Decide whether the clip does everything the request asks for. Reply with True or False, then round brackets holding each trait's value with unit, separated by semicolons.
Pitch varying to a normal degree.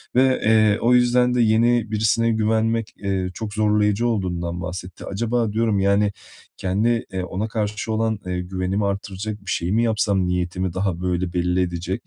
True (3.4 semitones)